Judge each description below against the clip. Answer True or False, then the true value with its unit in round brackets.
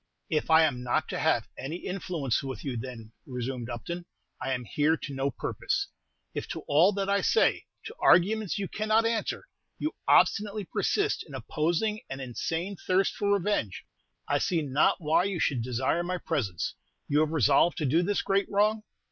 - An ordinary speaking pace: True (180 wpm)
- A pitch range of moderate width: False (7.0 semitones)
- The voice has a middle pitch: True (165 Hz)